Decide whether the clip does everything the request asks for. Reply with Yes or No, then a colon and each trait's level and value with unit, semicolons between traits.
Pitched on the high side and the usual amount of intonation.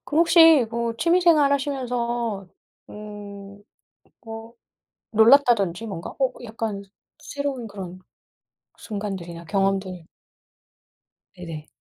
Yes: high, 225 Hz; average, 4.9 semitones